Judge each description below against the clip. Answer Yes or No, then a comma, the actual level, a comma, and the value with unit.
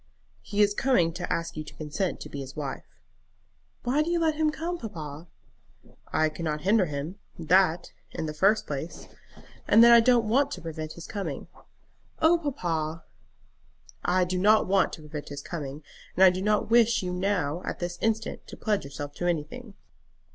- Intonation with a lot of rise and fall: Yes, wide, 5.9 semitones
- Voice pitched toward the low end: No, medium, 180 Hz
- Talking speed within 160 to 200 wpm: Yes, average, 185 wpm